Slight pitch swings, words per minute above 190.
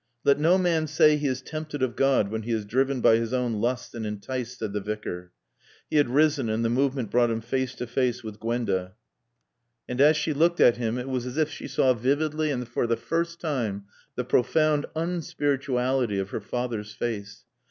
No: average, 4.3 semitones; fast, 205 wpm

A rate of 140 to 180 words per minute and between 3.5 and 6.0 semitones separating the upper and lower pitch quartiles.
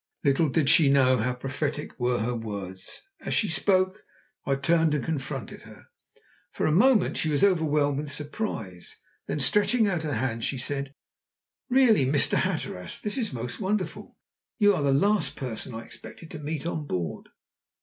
Yes: average, 170 wpm; average, 5.0 semitones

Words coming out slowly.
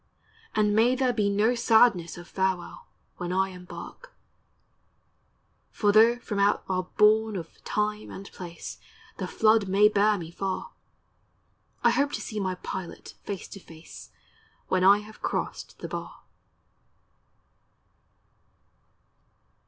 Yes: slow, 130 wpm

